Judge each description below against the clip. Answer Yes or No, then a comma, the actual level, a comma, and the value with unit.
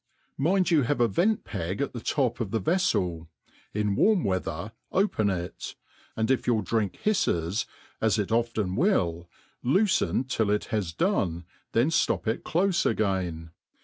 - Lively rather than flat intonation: Yes, wide, 8.6 semitones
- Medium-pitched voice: No, low, 110 Hz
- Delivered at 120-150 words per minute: Yes, average, 140 wpm